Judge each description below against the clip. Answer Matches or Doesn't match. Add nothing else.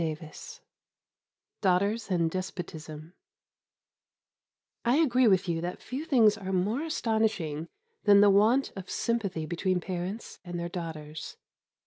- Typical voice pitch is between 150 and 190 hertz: Matches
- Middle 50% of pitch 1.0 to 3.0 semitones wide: Doesn't match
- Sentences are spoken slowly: Matches